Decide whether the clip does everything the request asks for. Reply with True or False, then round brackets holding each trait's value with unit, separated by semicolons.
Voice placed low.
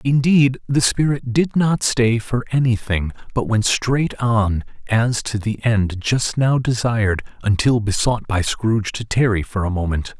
True (115 Hz)